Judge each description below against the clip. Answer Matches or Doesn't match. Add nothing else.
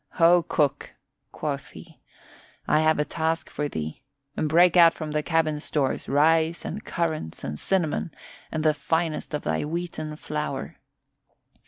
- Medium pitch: Matches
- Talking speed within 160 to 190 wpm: Doesn't match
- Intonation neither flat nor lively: Doesn't match